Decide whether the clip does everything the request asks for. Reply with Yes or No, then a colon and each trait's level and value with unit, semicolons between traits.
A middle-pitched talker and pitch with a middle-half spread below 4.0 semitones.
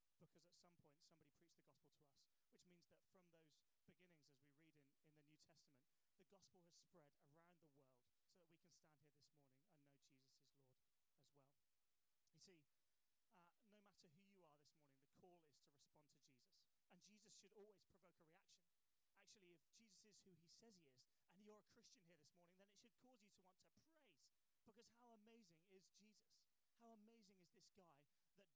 No: medium, 170 Hz; average, 5.2 semitones